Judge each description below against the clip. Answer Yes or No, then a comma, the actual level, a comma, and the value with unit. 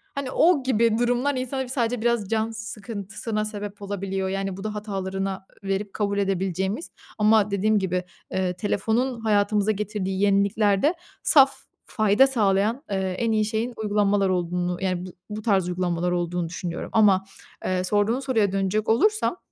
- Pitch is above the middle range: Yes, high, 205 Hz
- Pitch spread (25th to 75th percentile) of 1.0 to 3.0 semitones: Yes, average, 2.7 semitones